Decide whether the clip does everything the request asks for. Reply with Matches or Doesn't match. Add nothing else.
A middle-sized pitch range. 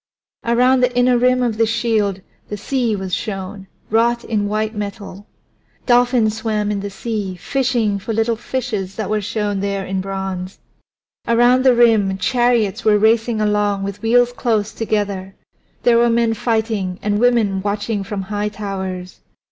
Matches